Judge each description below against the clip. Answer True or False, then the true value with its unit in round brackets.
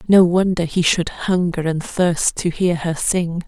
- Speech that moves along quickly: False (190 wpm)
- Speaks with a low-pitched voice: False (175 Hz)